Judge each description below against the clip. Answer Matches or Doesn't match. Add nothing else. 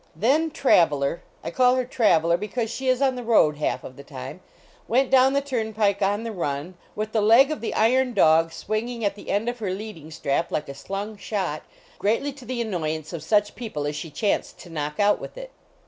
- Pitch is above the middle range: Matches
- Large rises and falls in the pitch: Matches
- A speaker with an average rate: Doesn't match